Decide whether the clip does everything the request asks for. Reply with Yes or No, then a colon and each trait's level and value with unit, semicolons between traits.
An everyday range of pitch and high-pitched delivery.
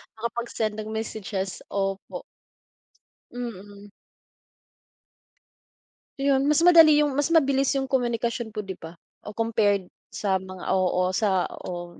Yes: average, 4.5 semitones; high, 215 Hz